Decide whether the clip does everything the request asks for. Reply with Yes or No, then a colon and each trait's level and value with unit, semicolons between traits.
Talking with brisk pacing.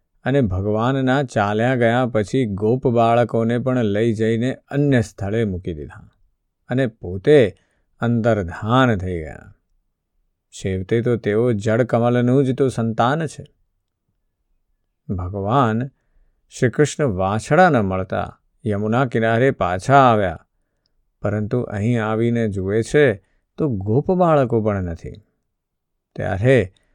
No: average, 105 wpm